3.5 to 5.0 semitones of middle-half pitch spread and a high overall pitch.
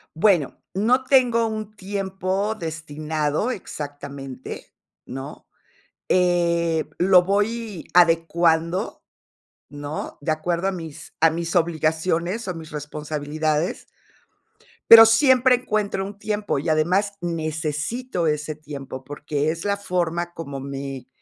No: average, 4.6 semitones; medium, 170 Hz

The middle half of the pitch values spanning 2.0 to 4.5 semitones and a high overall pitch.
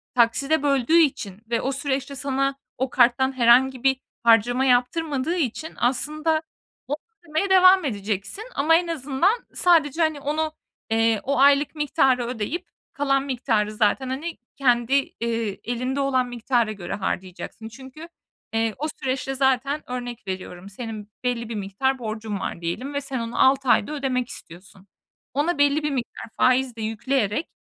Yes: average, 3.7 semitones; very high, 260 Hz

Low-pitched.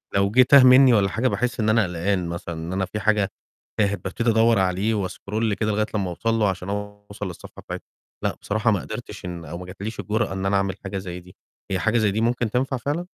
Yes: low, 105 Hz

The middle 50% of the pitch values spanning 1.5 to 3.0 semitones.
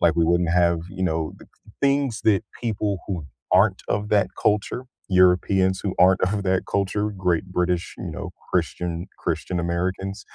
Yes: narrow, 2.4 semitones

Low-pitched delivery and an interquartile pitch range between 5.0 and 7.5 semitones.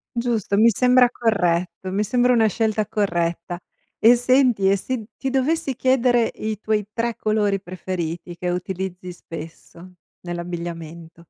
No: high, 205 Hz; average, 5.3 semitones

